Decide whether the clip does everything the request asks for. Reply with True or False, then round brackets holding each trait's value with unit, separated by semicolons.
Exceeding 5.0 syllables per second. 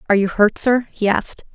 True (6.4 syllables/s)